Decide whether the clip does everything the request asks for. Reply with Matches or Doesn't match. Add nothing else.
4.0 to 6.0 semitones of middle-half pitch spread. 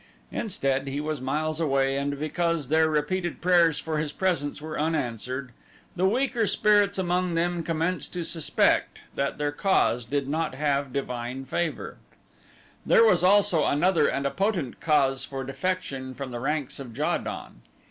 Matches